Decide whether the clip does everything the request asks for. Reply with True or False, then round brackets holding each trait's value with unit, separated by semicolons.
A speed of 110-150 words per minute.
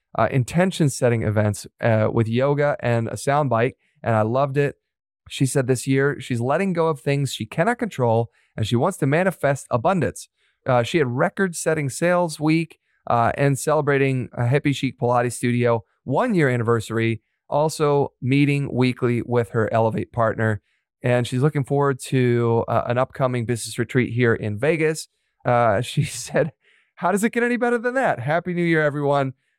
False (175 wpm)